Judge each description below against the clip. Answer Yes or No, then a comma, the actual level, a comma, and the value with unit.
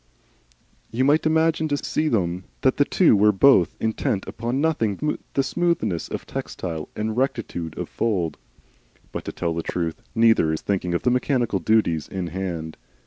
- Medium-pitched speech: No, low, 110 Hz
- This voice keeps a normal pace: Yes, average, 165 wpm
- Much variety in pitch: Yes, wide, 7.6 semitones